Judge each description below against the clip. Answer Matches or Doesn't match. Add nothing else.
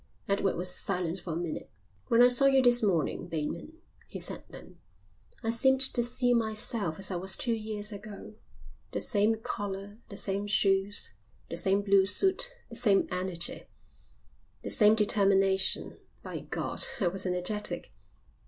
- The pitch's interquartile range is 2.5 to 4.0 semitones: Matches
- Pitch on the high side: Matches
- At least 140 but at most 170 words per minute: Matches